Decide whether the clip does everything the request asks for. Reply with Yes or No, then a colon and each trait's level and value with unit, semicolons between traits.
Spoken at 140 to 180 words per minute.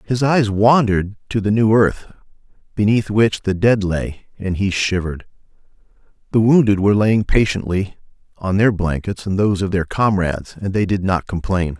Yes: average, 170 wpm